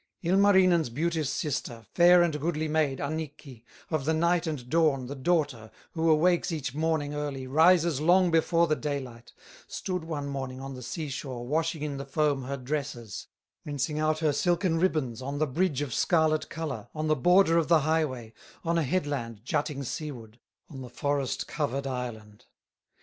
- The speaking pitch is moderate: Yes, medium, 150 Hz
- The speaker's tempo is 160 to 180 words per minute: Yes, average, 170 wpm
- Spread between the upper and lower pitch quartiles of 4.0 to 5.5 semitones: No, average, 3.5 semitones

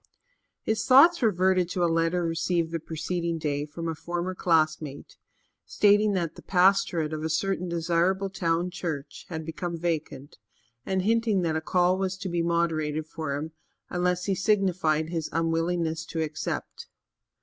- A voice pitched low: No, medium, 170 Hz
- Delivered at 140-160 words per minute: Yes, average, 155 wpm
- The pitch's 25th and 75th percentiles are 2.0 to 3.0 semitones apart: Yes, narrow, 2.6 semitones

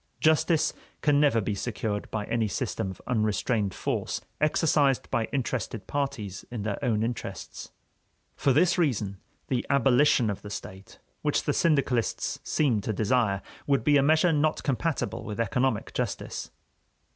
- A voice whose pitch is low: Yes, low, 120 Hz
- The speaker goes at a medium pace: Yes, average, 145 wpm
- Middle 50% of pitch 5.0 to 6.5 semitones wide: Yes, average, 5.3 semitones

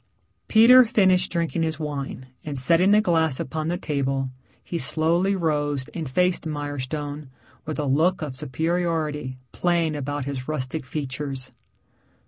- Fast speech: No, slow, 135 wpm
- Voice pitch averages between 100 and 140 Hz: No, medium, 155 Hz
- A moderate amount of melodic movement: Yes, average, 3.5 semitones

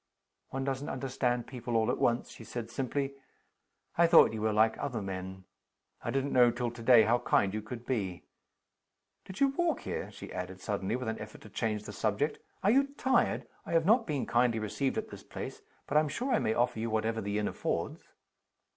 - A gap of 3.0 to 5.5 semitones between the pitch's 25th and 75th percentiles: Yes, average, 4.3 semitones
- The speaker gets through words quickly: Yes, fast, 210 wpm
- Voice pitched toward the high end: No, low, 120 Hz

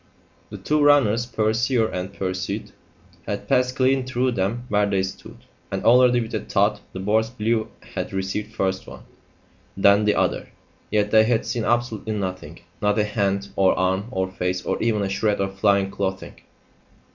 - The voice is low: Yes, low, 105 Hz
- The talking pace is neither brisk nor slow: Yes, average, 170 wpm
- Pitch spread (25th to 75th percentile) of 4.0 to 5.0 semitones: No, average, 3.3 semitones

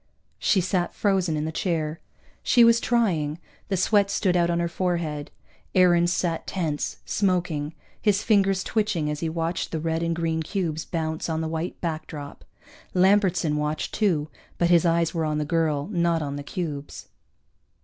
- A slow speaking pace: No, average, 170 wpm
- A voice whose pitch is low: No, medium, 170 Hz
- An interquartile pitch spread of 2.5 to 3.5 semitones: Yes, average, 2.8 semitones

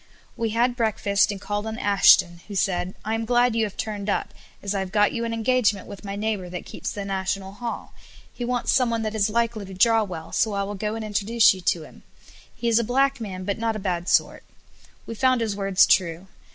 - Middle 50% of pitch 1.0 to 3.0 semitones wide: Yes, average, 2.7 semitones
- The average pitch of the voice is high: Yes, high, 210 Hz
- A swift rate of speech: Yes, fast, 230 wpm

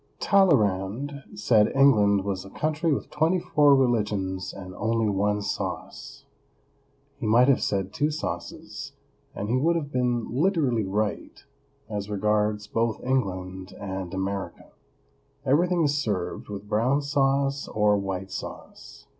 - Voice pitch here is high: No, low, 110 Hz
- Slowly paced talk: Yes, slow, 130 wpm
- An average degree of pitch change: No, wide, 5.9 semitones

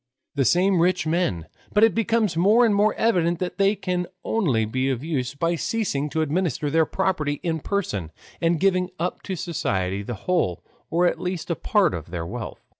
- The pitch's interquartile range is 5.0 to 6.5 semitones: Yes, wide, 5.5 semitones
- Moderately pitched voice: Yes, medium, 170 Hz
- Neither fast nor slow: Yes, average, 190 wpm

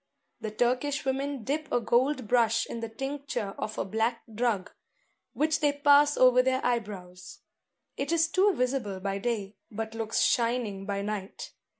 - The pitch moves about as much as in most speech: Yes, average, 4.5 semitones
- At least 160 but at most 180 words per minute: Yes, average, 165 wpm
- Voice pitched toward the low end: No, high, 240 Hz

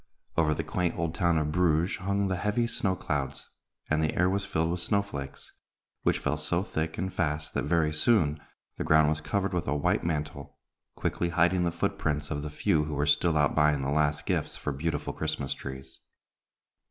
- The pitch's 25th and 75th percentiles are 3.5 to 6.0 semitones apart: No, average, 3.0 semitones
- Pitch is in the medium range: No, very low, 80 Hz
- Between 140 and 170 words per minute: No, average, 200 wpm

